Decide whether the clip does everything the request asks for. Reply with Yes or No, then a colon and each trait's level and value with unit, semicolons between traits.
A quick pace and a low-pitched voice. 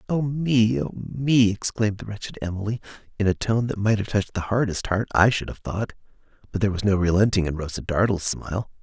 Yes: fast, 210 wpm; low, 105 Hz